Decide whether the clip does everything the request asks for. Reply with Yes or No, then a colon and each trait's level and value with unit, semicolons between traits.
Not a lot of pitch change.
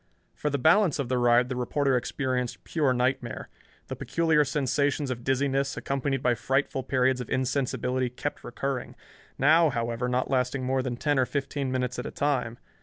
Yes: narrow, 2.1 semitones